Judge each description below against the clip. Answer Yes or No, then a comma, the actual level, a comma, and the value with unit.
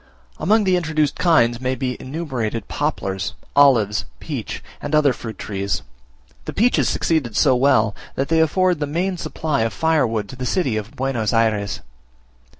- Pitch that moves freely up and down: Yes, wide, 6.1 semitones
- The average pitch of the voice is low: Yes, low, 130 Hz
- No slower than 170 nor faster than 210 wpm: No, average, 155 wpm